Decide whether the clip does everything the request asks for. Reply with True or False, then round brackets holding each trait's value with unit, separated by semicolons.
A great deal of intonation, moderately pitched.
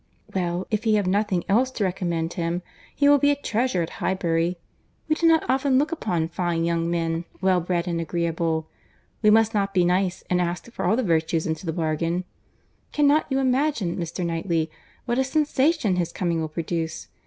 True (5.8 semitones; 180 Hz)